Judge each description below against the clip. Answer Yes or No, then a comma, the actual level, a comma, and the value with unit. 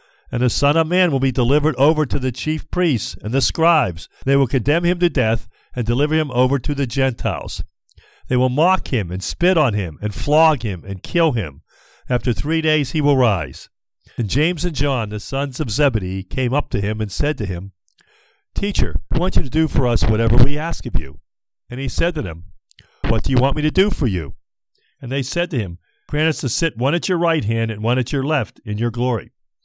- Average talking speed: No, fast, 230 wpm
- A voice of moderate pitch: No, low, 130 Hz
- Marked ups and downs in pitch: Yes, wide, 6.1 semitones